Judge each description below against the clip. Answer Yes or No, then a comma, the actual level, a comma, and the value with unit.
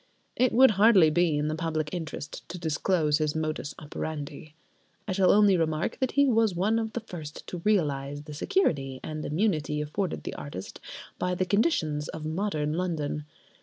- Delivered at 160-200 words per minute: Yes, average, 170 wpm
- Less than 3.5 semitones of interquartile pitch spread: No, average, 4.7 semitones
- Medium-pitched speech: Yes, medium, 160 Hz